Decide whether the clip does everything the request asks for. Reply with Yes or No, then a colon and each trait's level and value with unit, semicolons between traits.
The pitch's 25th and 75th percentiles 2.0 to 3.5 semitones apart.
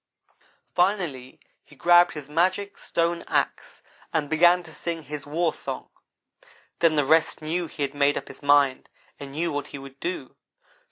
Yes: average, 3.2 semitones